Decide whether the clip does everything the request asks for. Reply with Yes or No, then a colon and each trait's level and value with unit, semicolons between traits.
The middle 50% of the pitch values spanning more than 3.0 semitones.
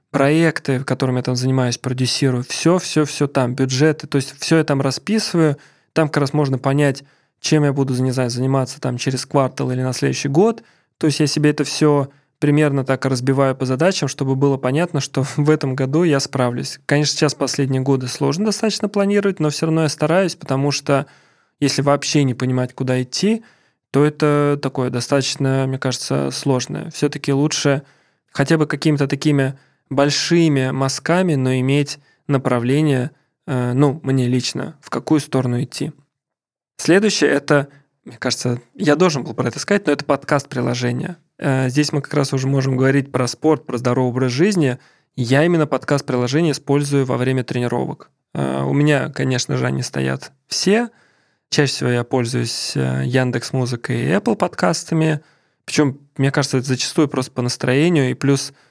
No: average, 2.7 semitones